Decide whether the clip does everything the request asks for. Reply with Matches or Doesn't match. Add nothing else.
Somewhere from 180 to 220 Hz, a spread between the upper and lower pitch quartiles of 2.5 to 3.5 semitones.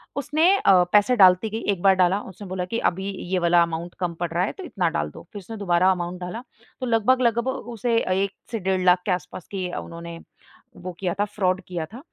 Doesn't match